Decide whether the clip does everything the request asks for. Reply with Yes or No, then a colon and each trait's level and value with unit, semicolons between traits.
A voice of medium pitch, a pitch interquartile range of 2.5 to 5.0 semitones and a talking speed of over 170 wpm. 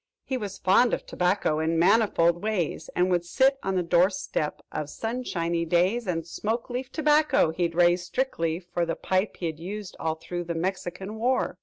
Yes: medium, 180 Hz; average, 4.4 semitones; average, 180 wpm